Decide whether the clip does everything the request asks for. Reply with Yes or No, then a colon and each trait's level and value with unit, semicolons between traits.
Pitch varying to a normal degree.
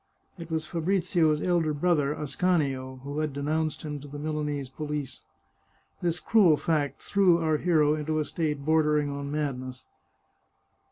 No: narrow, 2.1 semitones